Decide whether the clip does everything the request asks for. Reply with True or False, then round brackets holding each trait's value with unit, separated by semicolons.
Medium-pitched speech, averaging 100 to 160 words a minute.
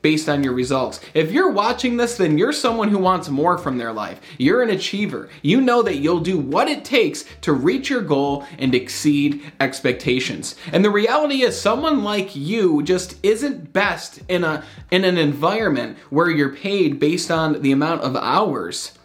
False (175 Hz; 185 wpm)